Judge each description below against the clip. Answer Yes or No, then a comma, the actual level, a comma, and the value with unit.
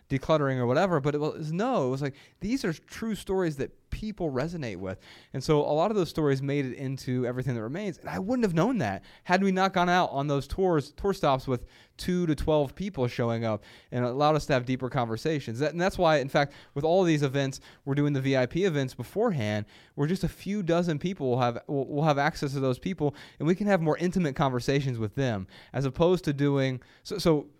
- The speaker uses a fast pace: Yes, fast, 235 wpm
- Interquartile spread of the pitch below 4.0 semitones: No, average, 5.0 semitones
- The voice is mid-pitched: Yes, medium, 145 Hz